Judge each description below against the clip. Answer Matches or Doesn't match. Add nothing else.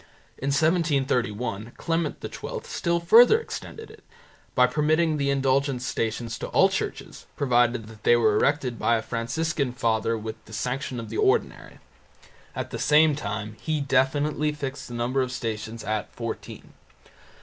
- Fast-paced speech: Doesn't match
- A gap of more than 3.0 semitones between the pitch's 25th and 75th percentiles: Matches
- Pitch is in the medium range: Doesn't match